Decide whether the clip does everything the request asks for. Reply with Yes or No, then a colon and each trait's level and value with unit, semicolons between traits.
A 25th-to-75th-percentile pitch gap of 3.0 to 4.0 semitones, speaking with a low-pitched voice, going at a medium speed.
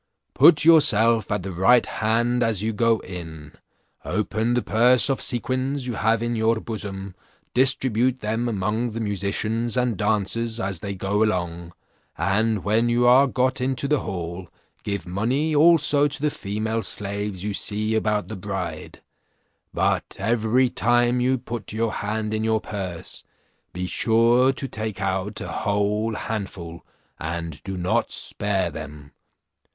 Yes: average, 3.6 semitones; low, 110 Hz; average, 150 wpm